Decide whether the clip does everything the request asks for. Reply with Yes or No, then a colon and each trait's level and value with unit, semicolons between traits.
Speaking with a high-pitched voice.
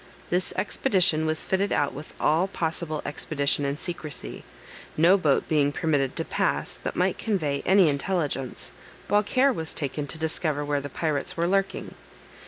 No: medium, 160 Hz